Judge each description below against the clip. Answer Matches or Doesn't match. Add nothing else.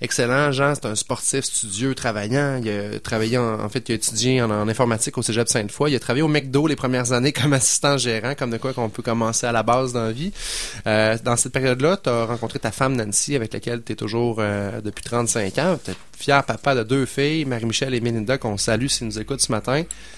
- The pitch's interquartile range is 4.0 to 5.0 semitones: Doesn't match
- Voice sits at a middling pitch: Doesn't match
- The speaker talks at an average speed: Doesn't match